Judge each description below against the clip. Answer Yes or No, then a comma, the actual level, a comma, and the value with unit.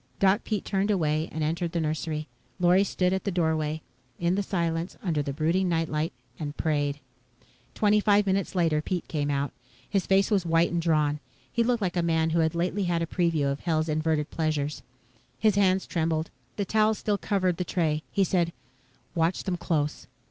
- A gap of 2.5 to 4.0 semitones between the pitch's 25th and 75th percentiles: Yes, average, 3.4 semitones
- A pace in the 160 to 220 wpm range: Yes, average, 190 wpm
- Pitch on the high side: No, medium, 170 Hz